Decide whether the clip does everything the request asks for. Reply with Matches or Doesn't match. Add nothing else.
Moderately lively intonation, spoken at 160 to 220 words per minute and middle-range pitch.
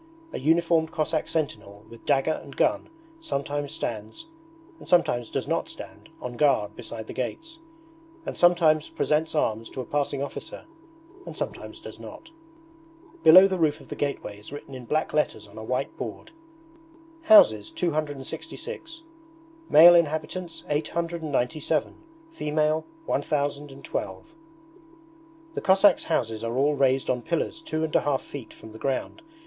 Doesn't match